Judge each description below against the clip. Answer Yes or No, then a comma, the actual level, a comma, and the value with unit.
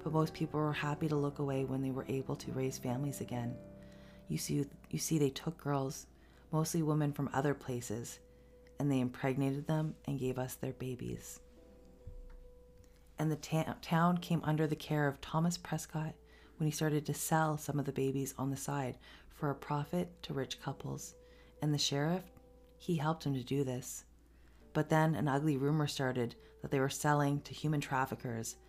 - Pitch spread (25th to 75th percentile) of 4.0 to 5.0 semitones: No, average, 3.2 semitones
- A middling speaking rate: Yes, average, 185 wpm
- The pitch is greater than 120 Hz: Yes, medium, 140 Hz